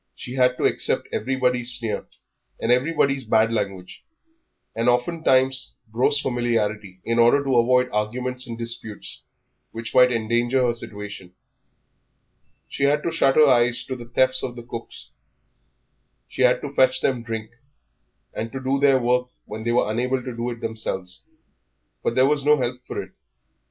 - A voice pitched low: Yes, low, 125 Hz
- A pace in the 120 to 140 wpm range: No, average, 160 wpm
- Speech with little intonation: Yes, narrow, 2.3 semitones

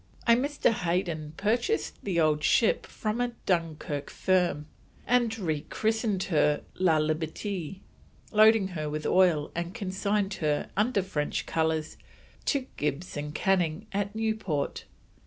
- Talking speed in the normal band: No, slow, 130 wpm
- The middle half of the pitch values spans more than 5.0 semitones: Yes, wide, 5.4 semitones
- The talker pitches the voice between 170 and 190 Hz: Yes, medium, 185 Hz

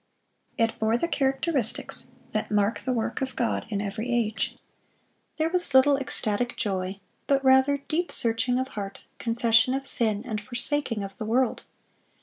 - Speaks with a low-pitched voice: No, high, 240 Hz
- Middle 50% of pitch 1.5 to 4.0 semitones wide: Yes, average, 3.6 semitones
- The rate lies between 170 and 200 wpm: No, average, 155 wpm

